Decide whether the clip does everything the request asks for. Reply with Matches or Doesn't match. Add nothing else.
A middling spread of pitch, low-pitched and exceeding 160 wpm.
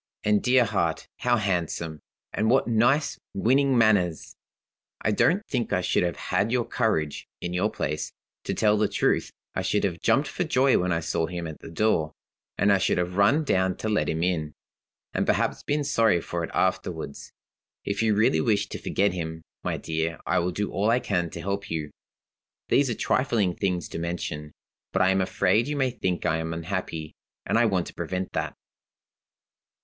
Matches